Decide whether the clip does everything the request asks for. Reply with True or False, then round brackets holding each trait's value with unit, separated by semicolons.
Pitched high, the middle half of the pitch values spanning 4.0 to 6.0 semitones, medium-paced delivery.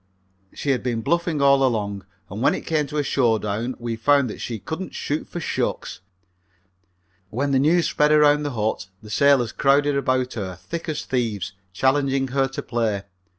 False (135 Hz; 4.4 semitones; 180 wpm)